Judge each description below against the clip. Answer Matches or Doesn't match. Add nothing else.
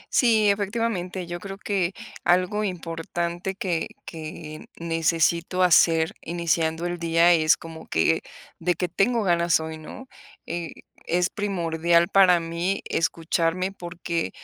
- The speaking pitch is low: Doesn't match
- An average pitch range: Doesn't match